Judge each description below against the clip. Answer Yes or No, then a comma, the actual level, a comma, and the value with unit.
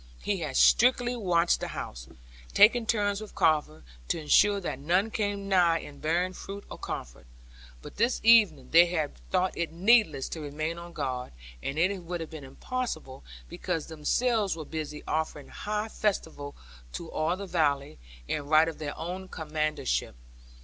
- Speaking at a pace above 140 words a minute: Yes, average, 165 wpm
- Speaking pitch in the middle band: Yes, medium, 170 Hz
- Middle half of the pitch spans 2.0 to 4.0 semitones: No, average, 4.8 semitones